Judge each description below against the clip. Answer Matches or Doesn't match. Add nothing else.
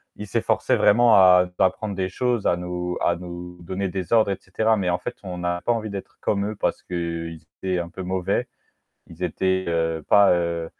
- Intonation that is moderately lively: Doesn't match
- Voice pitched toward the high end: Doesn't match